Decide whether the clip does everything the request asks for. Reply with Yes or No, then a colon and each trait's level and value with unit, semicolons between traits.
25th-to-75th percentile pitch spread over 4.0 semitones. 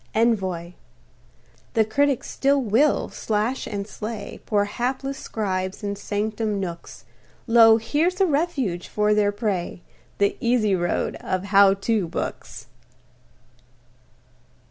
No: average, 3.2 semitones